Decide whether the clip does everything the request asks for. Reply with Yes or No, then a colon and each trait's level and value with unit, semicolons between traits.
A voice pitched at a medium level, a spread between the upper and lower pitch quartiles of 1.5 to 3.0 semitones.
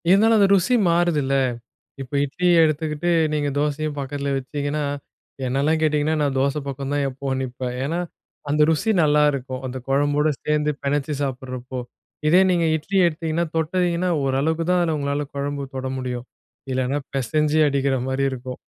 Yes: medium, 145 Hz; average, 2.7 semitones